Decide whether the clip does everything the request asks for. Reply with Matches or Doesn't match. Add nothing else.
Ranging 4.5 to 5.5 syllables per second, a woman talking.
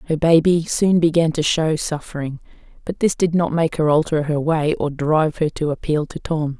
Matches